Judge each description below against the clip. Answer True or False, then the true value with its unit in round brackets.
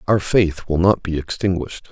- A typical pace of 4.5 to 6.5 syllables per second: True (5.1 syllables/s)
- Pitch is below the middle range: True (90 Hz)